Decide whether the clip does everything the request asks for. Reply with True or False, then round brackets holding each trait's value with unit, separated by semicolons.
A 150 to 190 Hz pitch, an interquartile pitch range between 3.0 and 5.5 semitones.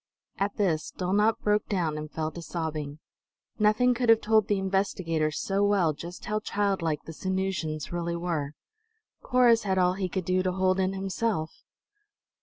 True (185 Hz; 3.7 semitones)